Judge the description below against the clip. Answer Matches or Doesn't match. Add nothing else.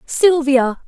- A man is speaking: Doesn't match